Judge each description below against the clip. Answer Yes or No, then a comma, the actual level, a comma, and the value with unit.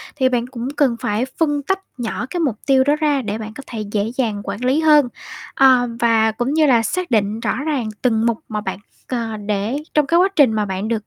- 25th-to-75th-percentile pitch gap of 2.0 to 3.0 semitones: No, average, 4.4 semitones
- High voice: Yes, high, 240 Hz